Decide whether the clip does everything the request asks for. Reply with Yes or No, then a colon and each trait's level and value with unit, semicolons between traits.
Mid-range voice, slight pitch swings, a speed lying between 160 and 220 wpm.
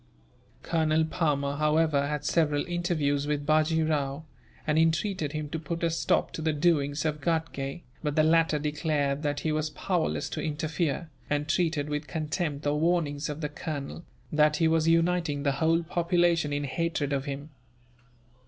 Yes: medium, 155 Hz; narrow, 2.0 semitones; average, 165 wpm